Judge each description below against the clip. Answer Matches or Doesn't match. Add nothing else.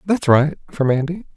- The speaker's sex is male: Matches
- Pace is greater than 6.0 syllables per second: Doesn't match